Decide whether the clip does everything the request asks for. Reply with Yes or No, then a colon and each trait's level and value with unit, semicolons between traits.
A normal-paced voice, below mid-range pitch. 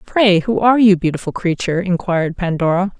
No: average, 160 wpm; medium, 185 Hz